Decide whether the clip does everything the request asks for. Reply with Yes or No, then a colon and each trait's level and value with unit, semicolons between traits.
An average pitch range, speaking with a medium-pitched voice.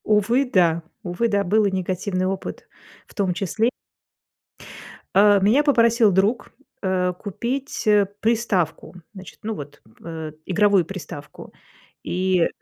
No: average, 3.2 semitones; high, 195 Hz